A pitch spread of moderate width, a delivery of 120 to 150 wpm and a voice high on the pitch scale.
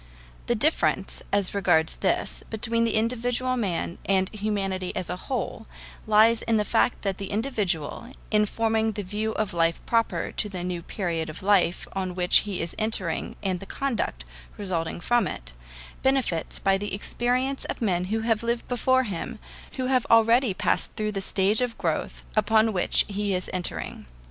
No: average, 3.8 semitones; average, 175 wpm; high, 210 Hz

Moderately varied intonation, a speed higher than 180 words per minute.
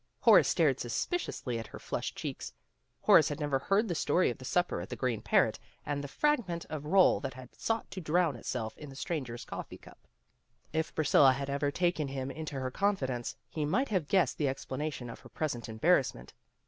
Yes: average, 4.9 semitones; average, 200 wpm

